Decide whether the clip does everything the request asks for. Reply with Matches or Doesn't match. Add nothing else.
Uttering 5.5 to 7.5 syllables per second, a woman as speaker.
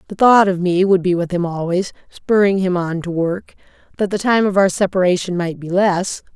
Doesn't match